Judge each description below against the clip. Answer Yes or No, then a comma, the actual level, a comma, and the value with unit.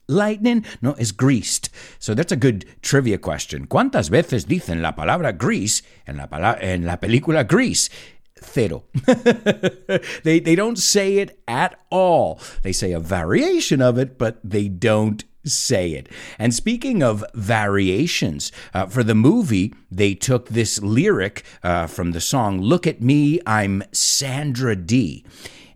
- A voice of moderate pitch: No, low, 120 Hz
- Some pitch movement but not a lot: No, wide, 8.5 semitones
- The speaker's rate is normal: Yes, average, 145 wpm